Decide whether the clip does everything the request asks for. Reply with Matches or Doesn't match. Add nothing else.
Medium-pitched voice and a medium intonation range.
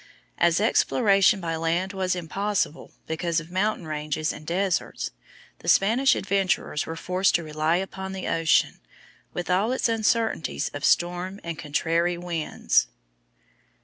Matches